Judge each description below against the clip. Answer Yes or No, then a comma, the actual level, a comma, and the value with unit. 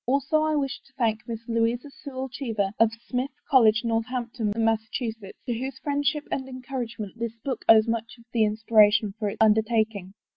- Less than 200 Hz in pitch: No, high, 230 Hz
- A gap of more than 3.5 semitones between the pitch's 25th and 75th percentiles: No, average, 3.0 semitones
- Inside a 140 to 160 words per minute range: No, average, 180 wpm